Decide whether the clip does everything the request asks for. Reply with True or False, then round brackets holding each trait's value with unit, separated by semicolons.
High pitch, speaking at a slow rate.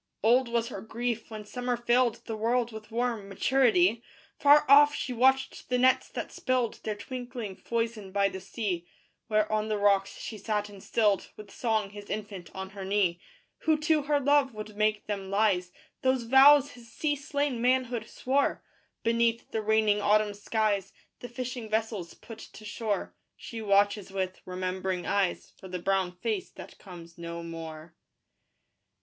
False (215 Hz; 165 wpm)